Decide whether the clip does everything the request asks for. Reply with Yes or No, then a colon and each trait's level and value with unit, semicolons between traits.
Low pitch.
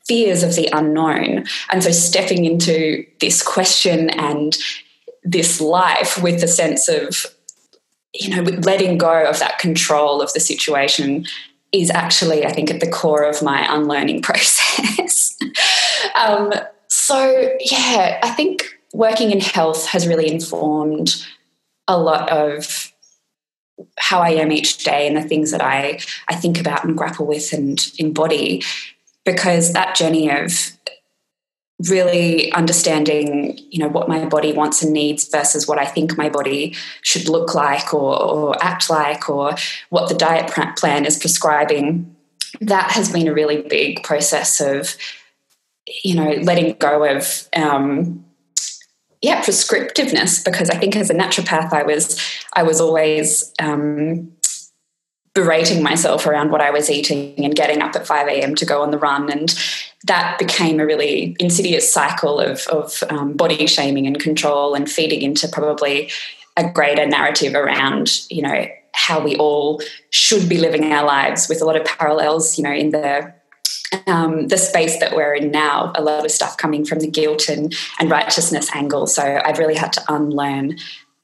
No: medium, 155 Hz